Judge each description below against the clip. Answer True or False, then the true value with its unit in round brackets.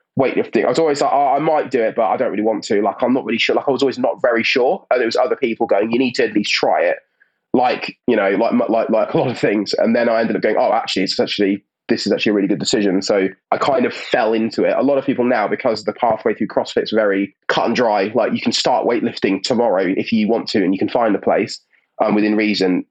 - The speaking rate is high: True (290 wpm)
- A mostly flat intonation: True (2.0 semitones)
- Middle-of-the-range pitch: False (105 Hz)